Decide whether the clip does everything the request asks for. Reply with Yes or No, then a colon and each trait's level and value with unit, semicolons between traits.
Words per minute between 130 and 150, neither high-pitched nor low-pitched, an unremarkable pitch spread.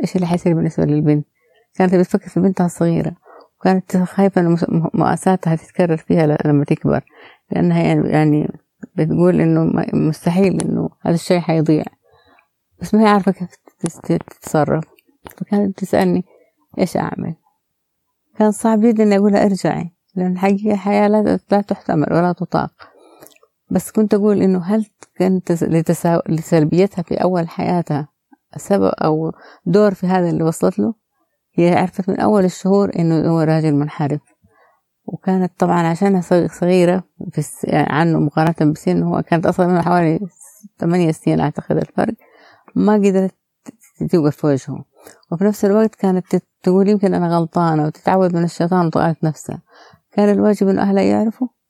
Yes: fast, 135 wpm; medium, 180 Hz; average, 3.5 semitones